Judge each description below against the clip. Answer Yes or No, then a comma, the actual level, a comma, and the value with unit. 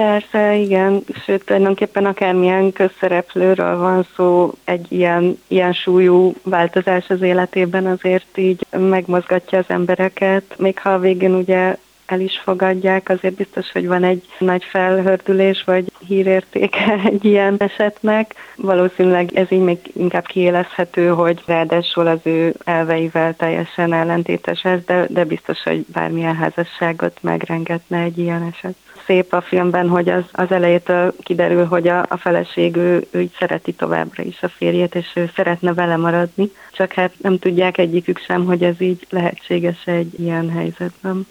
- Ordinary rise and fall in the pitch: No, narrow, 1.4 semitones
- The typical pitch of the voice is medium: Yes, medium, 180 Hz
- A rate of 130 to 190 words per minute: Yes, average, 150 wpm